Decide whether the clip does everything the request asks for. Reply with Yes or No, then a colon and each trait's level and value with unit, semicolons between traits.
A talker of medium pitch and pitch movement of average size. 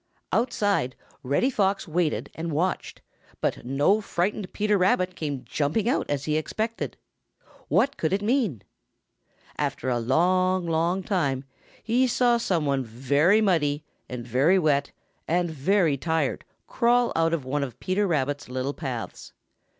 No: medium, 165 Hz; wide, 5.9 semitones